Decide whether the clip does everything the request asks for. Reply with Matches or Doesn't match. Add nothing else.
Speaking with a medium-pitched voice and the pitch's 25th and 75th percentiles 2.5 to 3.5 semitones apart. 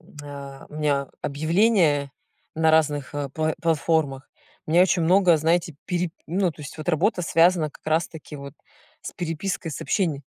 Matches